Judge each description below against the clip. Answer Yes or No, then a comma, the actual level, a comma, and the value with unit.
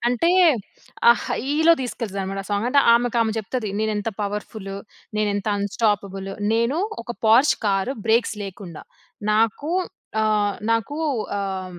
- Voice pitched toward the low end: No, high, 215 Hz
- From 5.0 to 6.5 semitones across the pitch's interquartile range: No, average, 2.9 semitones